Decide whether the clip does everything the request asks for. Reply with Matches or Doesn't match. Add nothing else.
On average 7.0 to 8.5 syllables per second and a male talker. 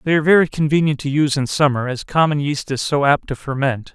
Doesn't match